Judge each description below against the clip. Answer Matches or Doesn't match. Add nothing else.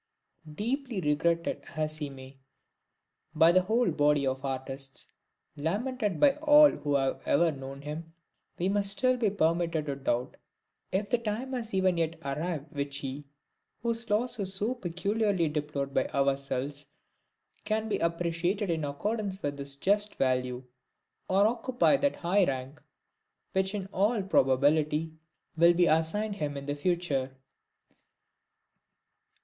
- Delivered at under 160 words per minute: Matches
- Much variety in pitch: Matches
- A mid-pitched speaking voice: Matches